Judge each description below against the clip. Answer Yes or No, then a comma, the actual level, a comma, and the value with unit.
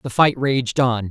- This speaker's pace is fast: Yes, fast, 215 wpm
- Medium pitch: No, low, 125 Hz